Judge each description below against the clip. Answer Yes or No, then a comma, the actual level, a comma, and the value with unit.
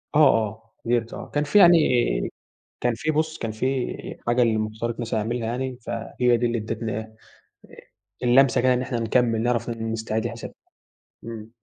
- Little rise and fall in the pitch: Yes, narrow, 1.9 semitones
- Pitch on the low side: Yes, low, 120 Hz